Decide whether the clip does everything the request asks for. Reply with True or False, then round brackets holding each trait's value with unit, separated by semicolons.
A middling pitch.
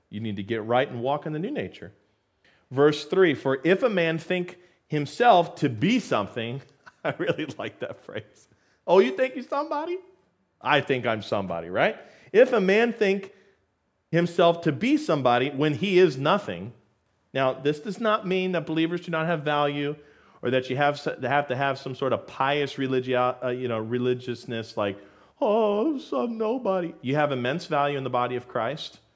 True (145 Hz)